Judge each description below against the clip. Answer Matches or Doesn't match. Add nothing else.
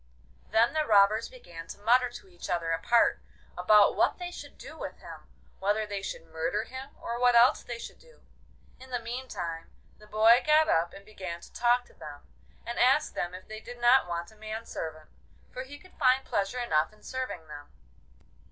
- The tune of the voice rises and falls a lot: Matches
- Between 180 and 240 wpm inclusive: Matches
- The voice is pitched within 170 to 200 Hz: Doesn't match